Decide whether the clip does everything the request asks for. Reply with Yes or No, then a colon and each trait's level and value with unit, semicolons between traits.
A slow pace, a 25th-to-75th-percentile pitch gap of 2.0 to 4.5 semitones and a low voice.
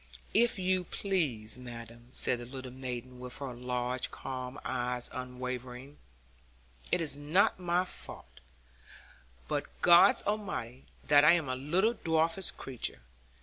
No: slow, 130 wpm; wide, 5.5 semitones; low, 130 Hz